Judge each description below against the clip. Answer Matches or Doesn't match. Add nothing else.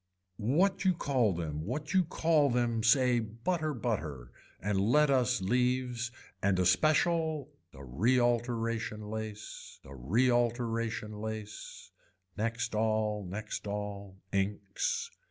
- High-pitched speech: Doesn't match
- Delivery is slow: Matches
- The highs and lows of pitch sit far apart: Doesn't match